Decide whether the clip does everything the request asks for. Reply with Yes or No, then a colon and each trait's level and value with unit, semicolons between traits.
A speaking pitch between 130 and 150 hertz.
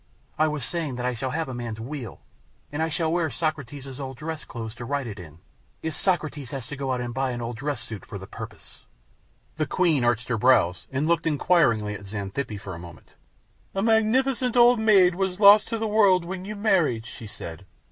Yes: medium, 140 Hz